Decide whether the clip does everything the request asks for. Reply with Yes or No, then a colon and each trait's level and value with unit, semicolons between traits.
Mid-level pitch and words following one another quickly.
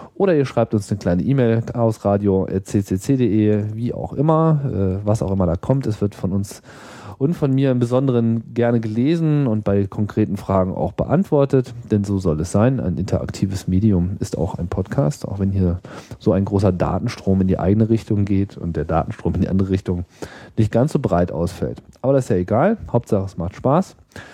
No: low, 105 Hz; fast, 195 wpm